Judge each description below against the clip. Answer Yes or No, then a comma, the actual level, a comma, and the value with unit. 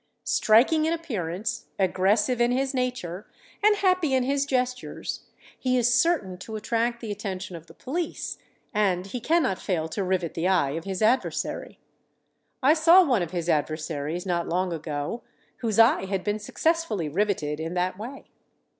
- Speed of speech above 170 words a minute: No, average, 165 wpm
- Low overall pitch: No, high, 210 Hz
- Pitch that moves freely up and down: Yes, wide, 6.1 semitones